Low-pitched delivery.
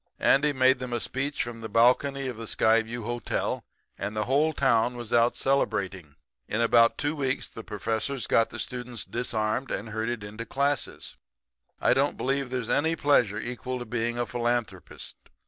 Yes: low, 120 Hz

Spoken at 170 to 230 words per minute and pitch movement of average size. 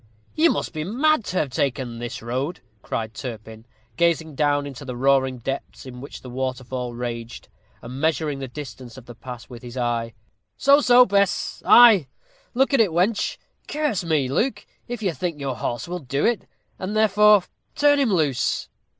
No: average, 175 wpm; wide, 8.1 semitones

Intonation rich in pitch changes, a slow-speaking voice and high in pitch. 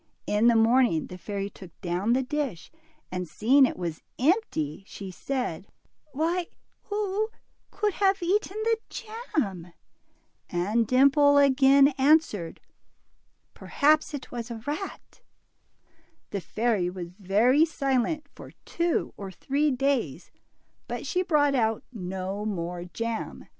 Yes: wide, 7.7 semitones; slow, 125 wpm; high, 245 Hz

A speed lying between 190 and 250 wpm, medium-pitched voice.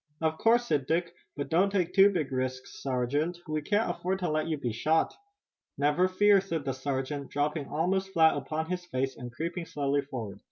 Yes: average, 195 wpm; medium, 155 Hz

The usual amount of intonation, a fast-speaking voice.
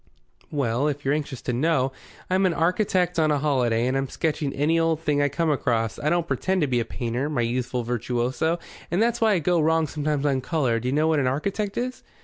Yes: average, 4.4 semitones; fast, 230 wpm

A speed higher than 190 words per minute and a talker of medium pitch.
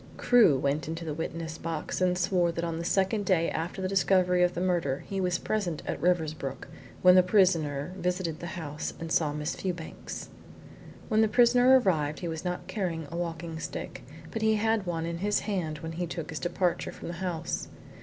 Yes: average, 200 wpm; medium, 175 Hz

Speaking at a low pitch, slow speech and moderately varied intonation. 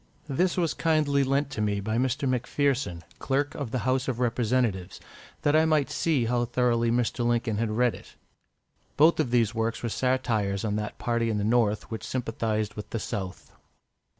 No: low, 120 Hz; average, 180 wpm; average, 3.4 semitones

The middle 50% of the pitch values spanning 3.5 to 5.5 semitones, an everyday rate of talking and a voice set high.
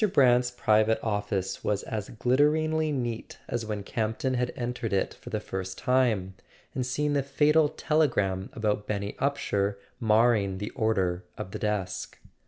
No: average, 4.1 semitones; average, 150 wpm; low, 110 Hz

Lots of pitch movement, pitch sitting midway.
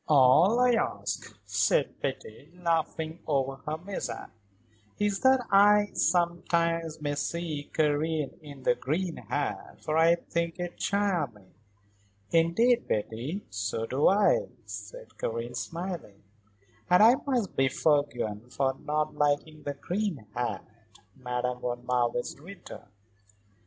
Yes: wide, 5.9 semitones; medium, 155 Hz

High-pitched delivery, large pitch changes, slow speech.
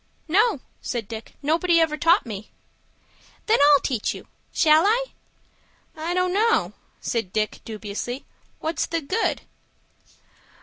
Yes: very high, 315 Hz; wide, 7.6 semitones; slow, 125 wpm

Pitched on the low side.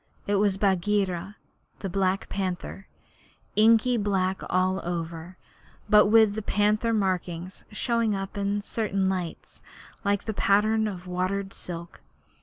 No: high, 195 Hz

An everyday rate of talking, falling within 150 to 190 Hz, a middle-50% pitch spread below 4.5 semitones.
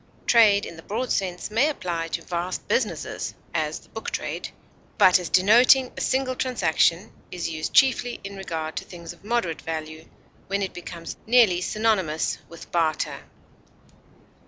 No: average, 155 wpm; medium, 185 Hz; wide, 5.4 semitones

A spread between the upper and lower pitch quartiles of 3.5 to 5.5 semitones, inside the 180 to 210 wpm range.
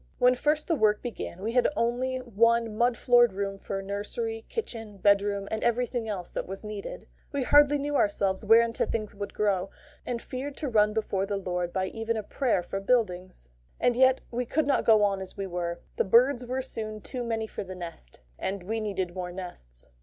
Yes: average, 4.1 semitones; average, 200 wpm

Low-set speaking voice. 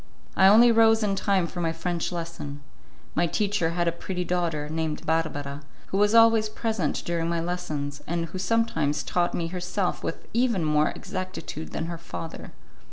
No: medium, 175 Hz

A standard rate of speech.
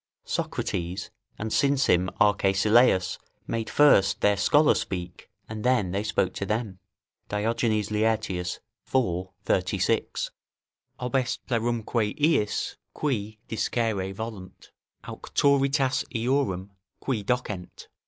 No: slow, 100 wpm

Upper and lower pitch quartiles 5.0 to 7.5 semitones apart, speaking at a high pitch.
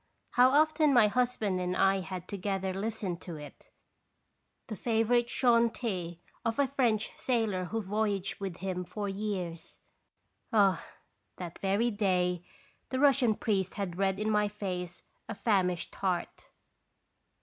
No: average, 3.6 semitones; high, 200 Hz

